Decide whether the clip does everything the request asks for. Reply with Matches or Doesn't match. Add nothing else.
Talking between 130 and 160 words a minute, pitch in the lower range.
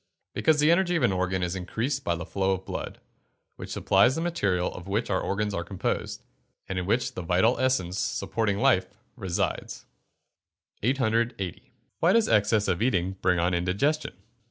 Doesn't match